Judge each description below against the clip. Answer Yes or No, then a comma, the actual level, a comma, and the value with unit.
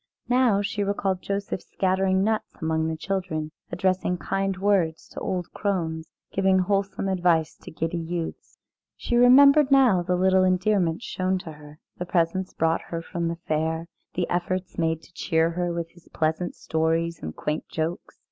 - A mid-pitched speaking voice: Yes, medium, 180 Hz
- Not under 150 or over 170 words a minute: Yes, average, 160 wpm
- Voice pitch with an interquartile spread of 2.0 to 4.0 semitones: Yes, average, 3.0 semitones